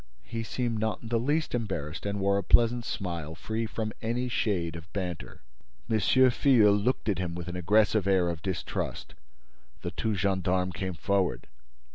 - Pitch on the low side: Yes, low, 100 Hz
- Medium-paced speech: Yes, average, 170 wpm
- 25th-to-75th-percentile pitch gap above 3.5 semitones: Yes, average, 4.0 semitones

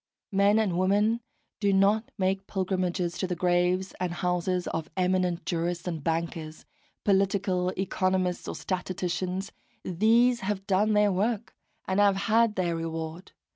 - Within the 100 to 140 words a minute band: Yes, slow, 135 wpm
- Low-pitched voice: No, medium, 185 Hz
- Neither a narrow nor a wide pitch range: No, narrow, 2.2 semitones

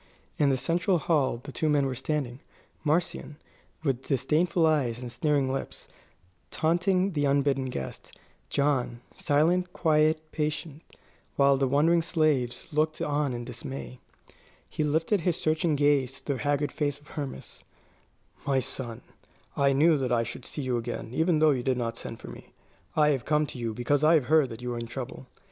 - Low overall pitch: No, medium, 145 Hz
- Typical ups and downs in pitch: Yes, average, 3.2 semitones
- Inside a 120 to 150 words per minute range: No, average, 175 wpm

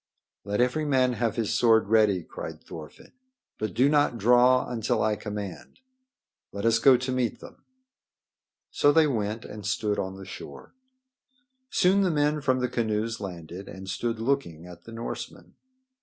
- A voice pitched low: Yes, low, 115 Hz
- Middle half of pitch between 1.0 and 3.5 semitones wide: No, average, 4.0 semitones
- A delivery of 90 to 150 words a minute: No, average, 160 wpm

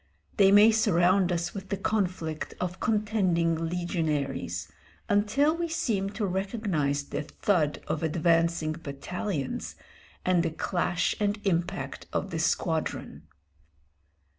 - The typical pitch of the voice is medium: Yes, medium, 180 Hz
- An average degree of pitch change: Yes, average, 4.0 semitones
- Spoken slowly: Yes, slow, 115 wpm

